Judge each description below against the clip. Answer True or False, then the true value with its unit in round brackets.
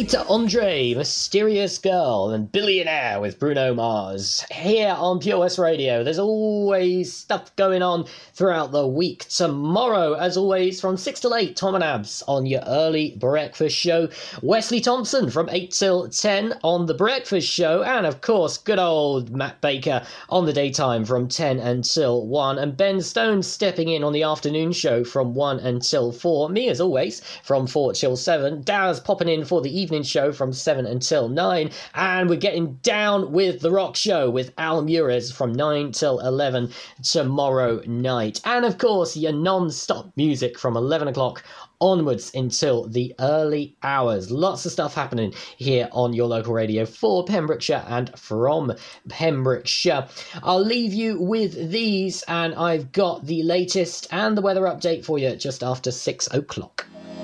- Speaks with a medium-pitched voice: True (160 Hz)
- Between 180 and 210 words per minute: False (165 wpm)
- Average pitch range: False (6.1 semitones)